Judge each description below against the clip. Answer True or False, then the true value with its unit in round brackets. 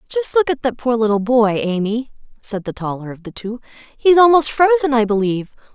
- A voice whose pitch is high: True (240 Hz)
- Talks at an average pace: False (210 wpm)